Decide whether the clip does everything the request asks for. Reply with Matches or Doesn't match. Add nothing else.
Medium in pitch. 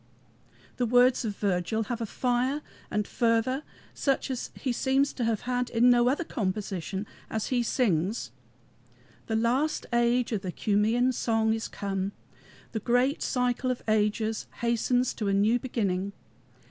Doesn't match